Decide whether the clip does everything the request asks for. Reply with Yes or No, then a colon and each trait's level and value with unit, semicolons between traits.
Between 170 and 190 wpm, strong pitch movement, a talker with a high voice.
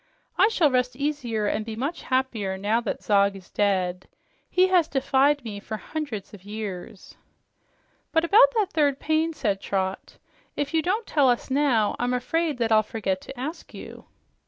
Yes: average, 175 wpm; wide, 6.5 semitones; very high, 250 Hz